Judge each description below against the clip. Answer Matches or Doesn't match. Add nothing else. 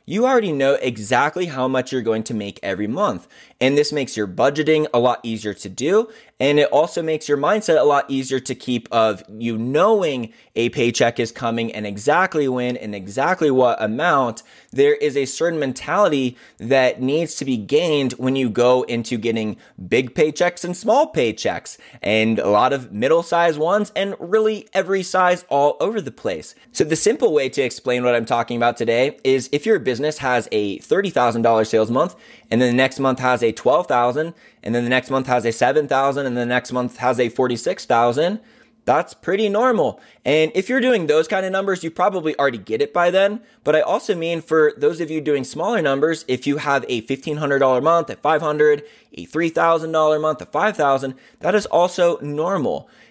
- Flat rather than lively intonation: Doesn't match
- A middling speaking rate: Matches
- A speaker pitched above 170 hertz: Doesn't match